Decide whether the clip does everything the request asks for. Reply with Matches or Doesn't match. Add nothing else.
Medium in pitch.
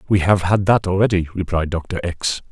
Doesn't match